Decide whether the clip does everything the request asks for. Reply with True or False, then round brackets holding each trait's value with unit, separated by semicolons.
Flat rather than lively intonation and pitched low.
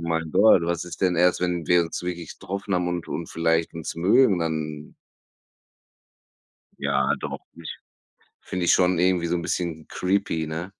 True (1.7 semitones; 85 Hz)